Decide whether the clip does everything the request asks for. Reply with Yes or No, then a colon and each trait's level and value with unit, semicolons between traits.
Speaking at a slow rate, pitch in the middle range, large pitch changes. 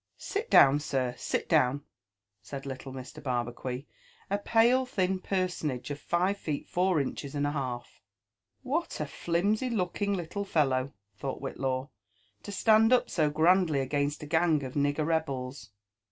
No: average, 155 wpm; medium, 150 Hz; wide, 5.8 semitones